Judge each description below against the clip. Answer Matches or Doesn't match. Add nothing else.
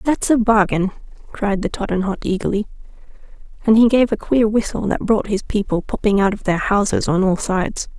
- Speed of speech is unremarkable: Matches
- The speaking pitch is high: Matches